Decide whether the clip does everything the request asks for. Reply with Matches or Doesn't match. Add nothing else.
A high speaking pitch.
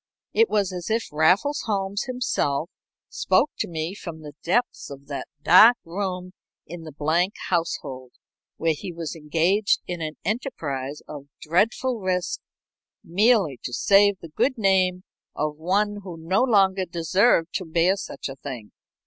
Doesn't match